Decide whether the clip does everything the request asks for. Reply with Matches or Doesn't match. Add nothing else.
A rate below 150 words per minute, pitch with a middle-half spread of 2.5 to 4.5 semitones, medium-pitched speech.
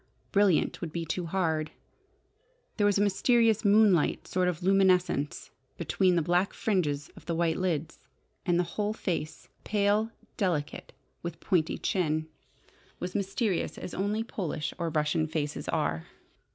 Matches